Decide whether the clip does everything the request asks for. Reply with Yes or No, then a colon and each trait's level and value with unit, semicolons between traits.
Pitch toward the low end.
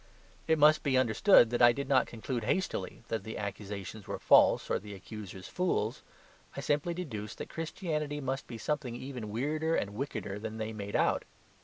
Yes: low, 120 Hz